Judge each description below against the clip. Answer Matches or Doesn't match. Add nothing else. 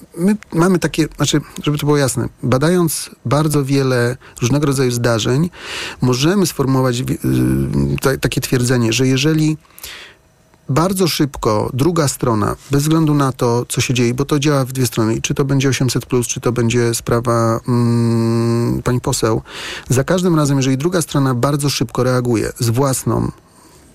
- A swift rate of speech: Doesn't match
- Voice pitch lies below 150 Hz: Matches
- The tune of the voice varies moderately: Matches